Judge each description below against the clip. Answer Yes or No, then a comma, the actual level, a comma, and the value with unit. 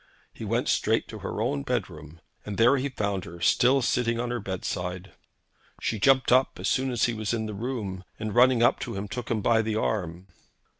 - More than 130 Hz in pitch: No, low, 110 Hz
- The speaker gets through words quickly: Yes, fast, 210 wpm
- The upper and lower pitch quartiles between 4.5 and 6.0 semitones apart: No, average, 4.1 semitones